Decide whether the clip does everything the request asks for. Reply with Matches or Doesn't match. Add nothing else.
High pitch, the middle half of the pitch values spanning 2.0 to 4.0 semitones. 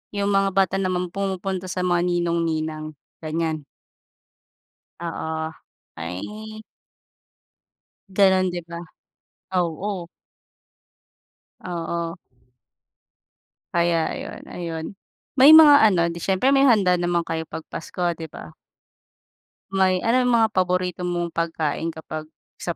Doesn't match